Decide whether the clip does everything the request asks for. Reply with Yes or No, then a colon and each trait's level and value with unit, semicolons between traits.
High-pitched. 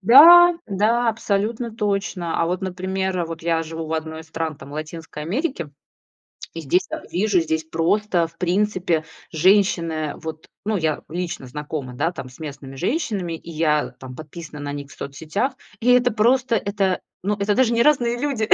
No: medium, 175 Hz